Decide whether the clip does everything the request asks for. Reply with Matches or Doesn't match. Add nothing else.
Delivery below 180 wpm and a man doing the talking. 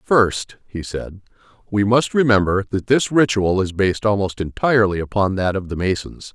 Matches